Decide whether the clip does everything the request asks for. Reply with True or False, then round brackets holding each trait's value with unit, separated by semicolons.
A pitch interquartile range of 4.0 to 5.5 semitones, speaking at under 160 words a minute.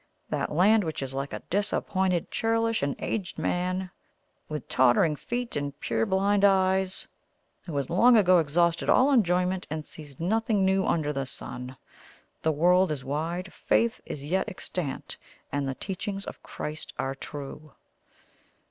True (4.8 semitones; 150 wpm)